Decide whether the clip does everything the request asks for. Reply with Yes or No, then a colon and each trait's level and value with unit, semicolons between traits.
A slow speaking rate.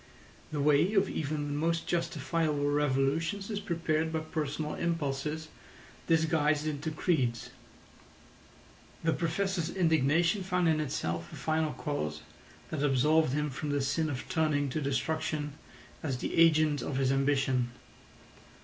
Yes: slow, 130 wpm